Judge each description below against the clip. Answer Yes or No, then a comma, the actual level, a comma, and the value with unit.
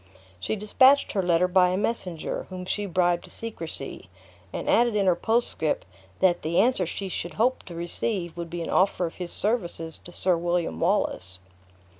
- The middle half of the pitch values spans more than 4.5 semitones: No, average, 3.3 semitones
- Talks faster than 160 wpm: Yes, average, 180 wpm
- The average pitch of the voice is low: No, medium, 180 Hz